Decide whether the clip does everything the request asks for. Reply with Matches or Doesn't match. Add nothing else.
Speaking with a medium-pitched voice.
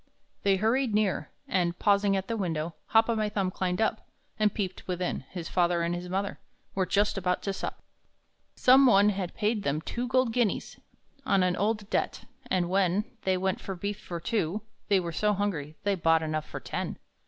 Doesn't match